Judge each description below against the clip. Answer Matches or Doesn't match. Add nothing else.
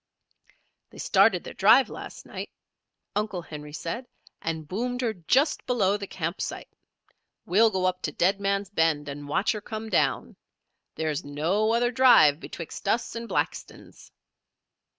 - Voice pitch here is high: Matches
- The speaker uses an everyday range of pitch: Doesn't match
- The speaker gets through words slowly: Doesn't match